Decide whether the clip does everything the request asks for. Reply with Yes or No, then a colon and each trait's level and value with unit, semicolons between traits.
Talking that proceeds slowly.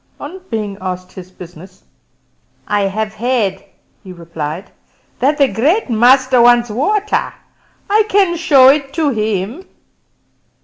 Yes: slow, 125 wpm